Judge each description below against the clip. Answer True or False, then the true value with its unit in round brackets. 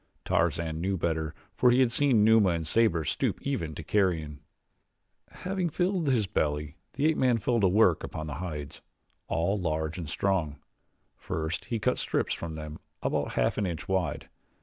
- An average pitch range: False (6.4 semitones)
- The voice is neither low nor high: False (90 Hz)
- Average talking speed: True (170 wpm)